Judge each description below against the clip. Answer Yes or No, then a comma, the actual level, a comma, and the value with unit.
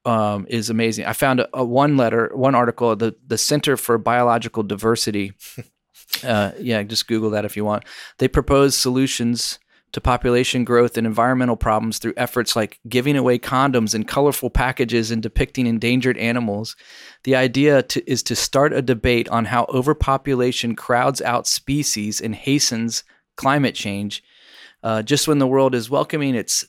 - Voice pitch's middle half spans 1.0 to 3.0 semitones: Yes, narrow, 2.4 semitones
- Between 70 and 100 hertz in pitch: No, low, 120 Hz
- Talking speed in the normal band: Yes, average, 165 wpm